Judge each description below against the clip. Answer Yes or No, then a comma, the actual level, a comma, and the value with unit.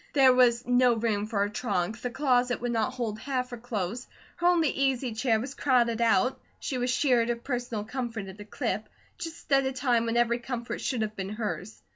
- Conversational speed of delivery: No, fast, 210 wpm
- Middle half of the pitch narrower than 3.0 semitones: Yes, narrow, 2.5 semitones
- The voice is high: Yes, high, 240 Hz